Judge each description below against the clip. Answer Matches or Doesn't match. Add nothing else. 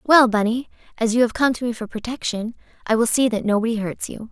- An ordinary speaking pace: Doesn't match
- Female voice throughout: Matches